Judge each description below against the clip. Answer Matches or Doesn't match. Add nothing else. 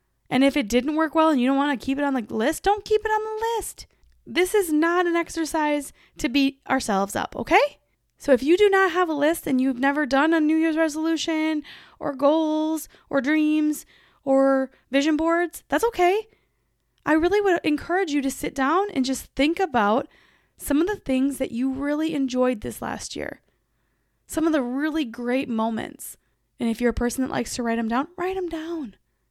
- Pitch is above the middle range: Matches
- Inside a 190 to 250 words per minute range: Matches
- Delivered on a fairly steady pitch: Doesn't match